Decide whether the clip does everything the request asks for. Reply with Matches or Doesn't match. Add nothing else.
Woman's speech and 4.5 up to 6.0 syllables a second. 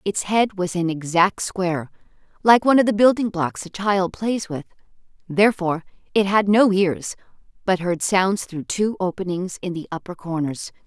Matches